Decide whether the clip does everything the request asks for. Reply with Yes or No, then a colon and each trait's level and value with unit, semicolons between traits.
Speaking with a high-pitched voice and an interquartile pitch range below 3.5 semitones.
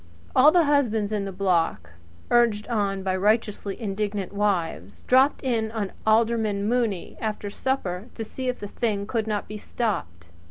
Yes: high, 210 Hz; average, 2.9 semitones